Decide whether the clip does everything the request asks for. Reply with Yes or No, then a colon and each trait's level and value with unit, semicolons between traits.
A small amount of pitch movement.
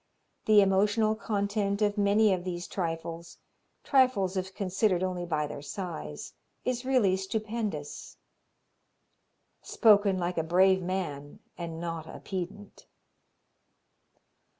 No: average, 3.1 semitones